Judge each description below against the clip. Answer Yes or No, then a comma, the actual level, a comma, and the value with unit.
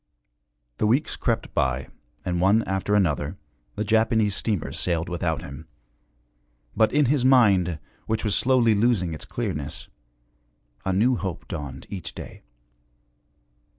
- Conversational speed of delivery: No, slow, 130 wpm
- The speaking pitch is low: Yes, low, 100 Hz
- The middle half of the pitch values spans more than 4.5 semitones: Yes, average, 4.9 semitones